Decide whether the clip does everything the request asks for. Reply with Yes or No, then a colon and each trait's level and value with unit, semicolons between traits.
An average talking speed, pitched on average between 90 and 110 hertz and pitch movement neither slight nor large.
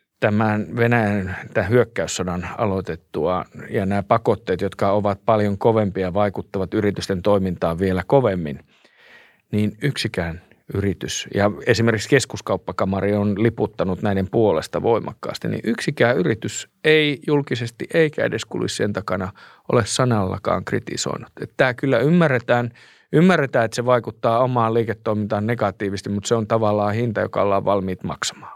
Yes: average, 130 wpm; low, 105 Hz; average, 3.2 semitones